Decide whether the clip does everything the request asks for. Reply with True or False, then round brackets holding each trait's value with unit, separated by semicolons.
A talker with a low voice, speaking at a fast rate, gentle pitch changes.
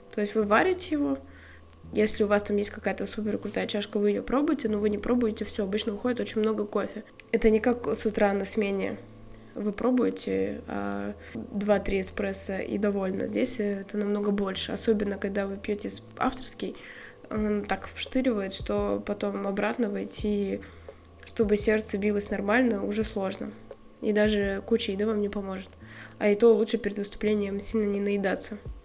False (205 Hz; 165 wpm; 1.8 semitones)